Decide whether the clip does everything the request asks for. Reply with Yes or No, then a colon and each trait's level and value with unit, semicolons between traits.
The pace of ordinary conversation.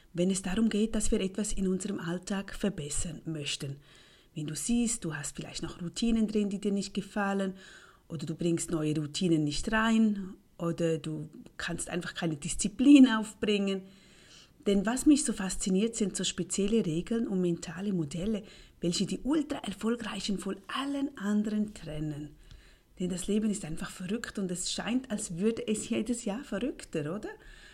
Yes: average, 160 wpm